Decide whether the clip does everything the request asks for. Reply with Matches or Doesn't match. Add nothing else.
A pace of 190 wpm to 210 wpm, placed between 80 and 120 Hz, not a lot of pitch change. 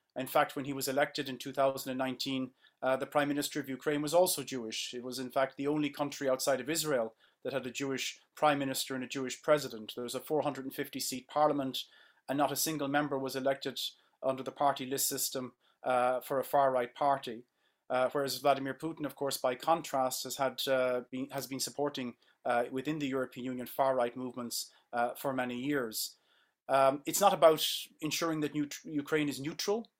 Doesn't match